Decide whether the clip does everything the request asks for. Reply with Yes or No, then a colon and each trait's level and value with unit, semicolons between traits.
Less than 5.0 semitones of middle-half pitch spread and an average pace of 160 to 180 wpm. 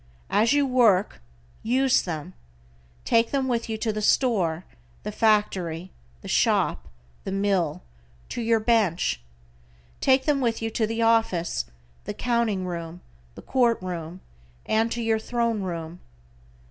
No: average, 4.5 semitones; average, 140 wpm